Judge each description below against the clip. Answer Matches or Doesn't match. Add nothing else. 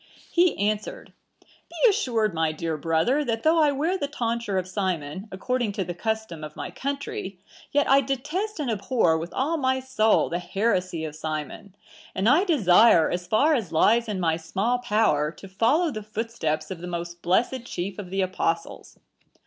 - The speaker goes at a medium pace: Matches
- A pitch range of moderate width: Doesn't match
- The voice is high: Matches